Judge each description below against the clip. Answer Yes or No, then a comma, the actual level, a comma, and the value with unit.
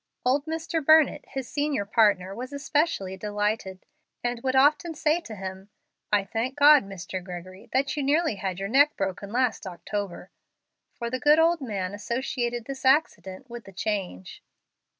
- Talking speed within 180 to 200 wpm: No, average, 160 wpm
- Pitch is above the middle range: Yes, high, 235 Hz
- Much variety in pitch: Yes, wide, 6.5 semitones